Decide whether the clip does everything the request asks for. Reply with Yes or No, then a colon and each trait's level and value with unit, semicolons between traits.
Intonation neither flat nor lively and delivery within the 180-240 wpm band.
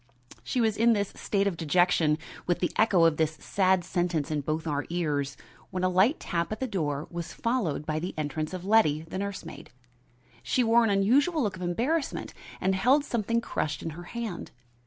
No: wide, 5.7 semitones; average, 200 wpm